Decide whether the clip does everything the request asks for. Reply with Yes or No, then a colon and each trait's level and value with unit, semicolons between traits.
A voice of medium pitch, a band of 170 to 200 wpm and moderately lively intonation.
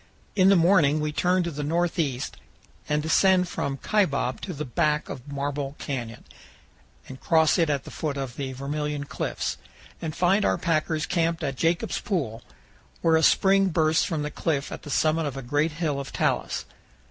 Yes: medium, 155 Hz; average, 180 wpm; average, 3.2 semitones